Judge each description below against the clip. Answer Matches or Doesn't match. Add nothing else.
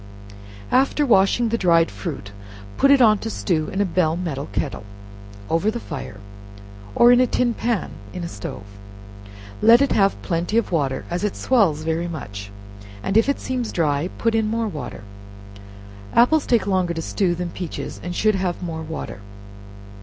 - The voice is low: Doesn't match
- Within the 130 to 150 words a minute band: Doesn't match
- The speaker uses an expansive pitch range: Matches